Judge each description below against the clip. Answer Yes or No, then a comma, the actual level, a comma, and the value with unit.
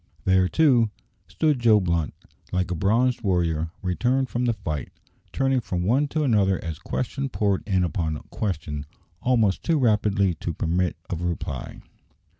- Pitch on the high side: No, low, 100 Hz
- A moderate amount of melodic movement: No, wide, 5.8 semitones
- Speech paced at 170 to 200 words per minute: No, average, 155 wpm